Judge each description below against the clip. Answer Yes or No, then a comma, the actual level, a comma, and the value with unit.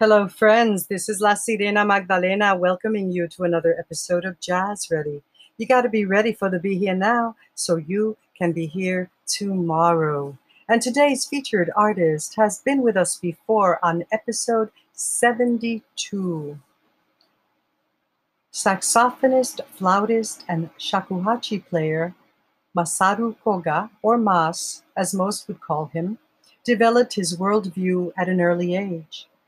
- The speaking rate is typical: No, slow, 130 wpm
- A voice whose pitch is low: No, high, 195 Hz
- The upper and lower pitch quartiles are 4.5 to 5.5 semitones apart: No, average, 4.1 semitones